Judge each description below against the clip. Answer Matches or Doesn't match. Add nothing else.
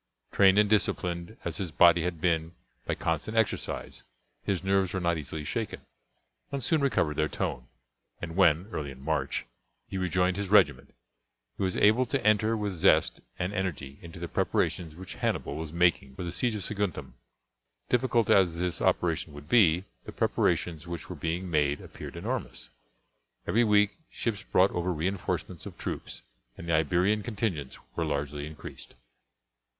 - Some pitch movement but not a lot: Matches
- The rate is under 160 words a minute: Doesn't match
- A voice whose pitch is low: Matches